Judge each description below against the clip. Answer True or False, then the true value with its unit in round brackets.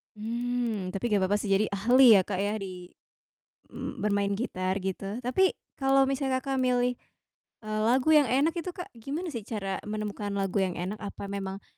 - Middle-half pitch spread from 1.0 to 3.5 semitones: False (4.5 semitones)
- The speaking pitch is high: True (215 Hz)